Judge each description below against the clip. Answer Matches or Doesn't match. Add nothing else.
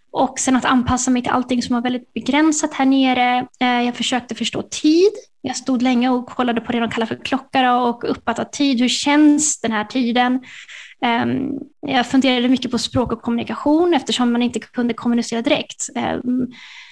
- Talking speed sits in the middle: Matches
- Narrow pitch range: Matches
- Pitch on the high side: Matches